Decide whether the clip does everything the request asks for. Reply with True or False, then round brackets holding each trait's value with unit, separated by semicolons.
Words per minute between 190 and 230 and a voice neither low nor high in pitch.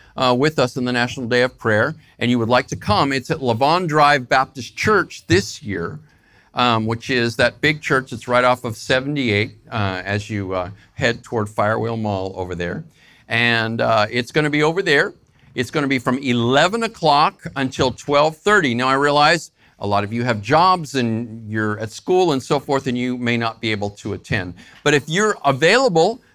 False (205 wpm; 125 Hz)